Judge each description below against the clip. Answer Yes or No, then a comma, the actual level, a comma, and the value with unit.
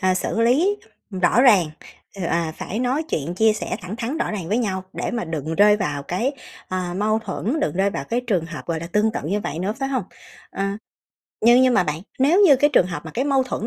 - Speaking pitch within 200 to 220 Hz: Yes, high, 210 Hz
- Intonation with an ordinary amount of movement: No, wide, 5.7 semitones